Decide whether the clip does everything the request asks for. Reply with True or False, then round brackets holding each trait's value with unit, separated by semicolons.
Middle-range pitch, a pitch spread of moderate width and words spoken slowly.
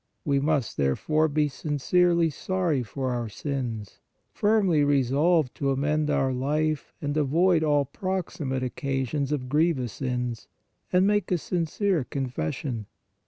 True (145 Hz; 3.9 semitones; 125 wpm)